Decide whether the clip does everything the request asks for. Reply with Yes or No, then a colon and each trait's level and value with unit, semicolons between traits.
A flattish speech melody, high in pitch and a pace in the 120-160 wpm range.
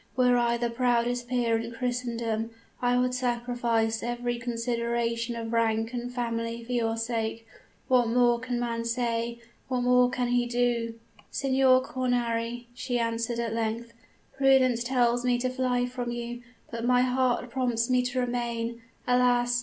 Yes: narrow, 1.2 semitones; high, 240 Hz; average, 155 wpm